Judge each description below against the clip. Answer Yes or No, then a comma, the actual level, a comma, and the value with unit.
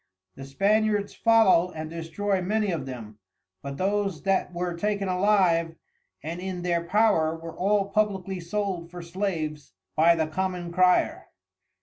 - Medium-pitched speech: Yes, medium, 180 Hz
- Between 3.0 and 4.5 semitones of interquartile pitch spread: Yes, average, 3.4 semitones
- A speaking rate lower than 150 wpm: Yes, average, 140 wpm